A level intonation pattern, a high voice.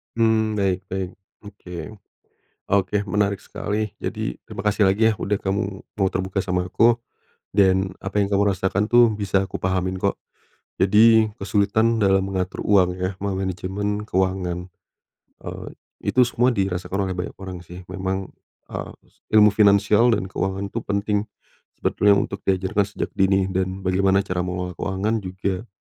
No: narrow, 1.8 semitones; very low, 95 Hz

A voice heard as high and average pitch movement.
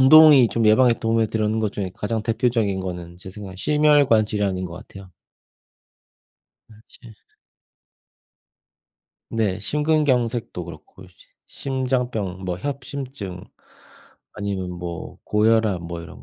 No: low, 110 Hz; average, 4.9 semitones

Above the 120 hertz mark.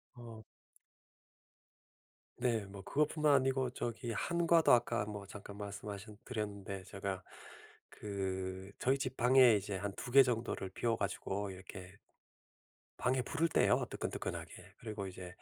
No: low, 105 Hz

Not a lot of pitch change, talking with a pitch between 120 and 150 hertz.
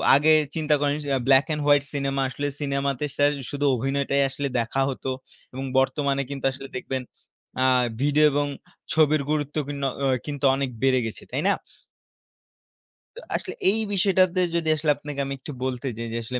Yes: narrow, 1.6 semitones; medium, 140 Hz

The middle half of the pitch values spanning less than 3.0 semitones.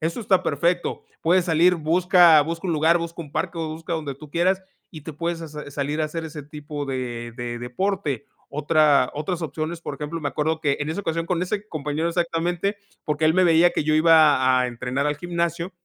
Yes: narrow, 2.6 semitones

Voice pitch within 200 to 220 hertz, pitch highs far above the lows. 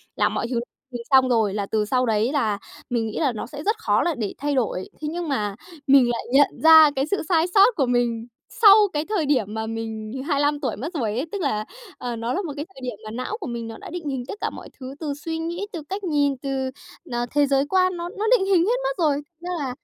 No: very high, 275 Hz; wide, 5.9 semitones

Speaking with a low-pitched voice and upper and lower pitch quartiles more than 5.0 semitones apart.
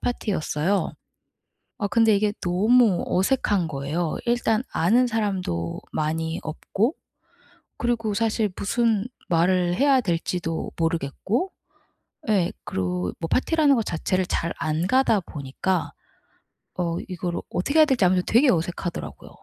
No: medium, 185 Hz; wide, 5.4 semitones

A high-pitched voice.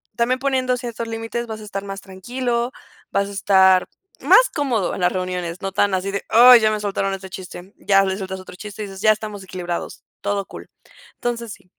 Yes: high, 200 Hz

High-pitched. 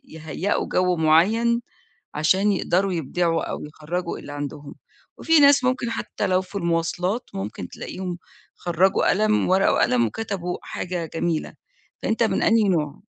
No: medium, 180 Hz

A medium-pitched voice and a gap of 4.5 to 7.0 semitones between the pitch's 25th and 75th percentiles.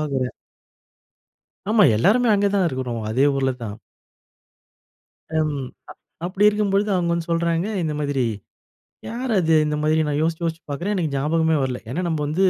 Yes: medium, 160 Hz; average, 5.1 semitones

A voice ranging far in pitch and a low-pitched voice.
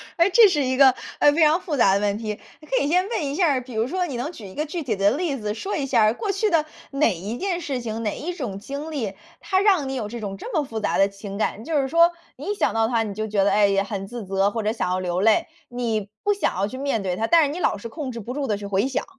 No: wide, 6.8 semitones; high, 245 Hz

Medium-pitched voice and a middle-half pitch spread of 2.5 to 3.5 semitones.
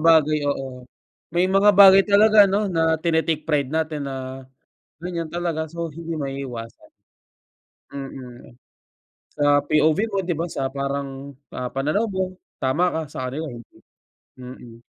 No: medium, 155 Hz; average, 4.2 semitones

